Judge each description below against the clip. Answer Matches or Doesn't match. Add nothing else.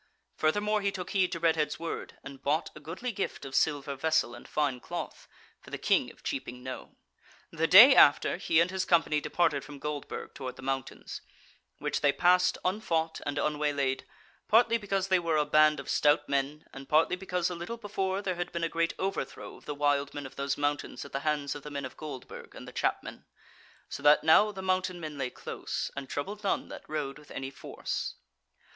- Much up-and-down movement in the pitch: Doesn't match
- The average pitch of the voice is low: Doesn't match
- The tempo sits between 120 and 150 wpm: Doesn't match